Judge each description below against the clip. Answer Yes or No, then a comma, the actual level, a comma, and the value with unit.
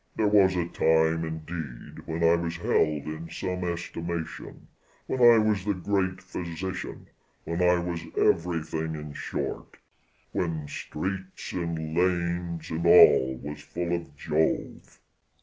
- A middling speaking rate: No, slow, 130 wpm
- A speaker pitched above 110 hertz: No, very low, 85 Hz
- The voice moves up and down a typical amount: No, narrow, 2.1 semitones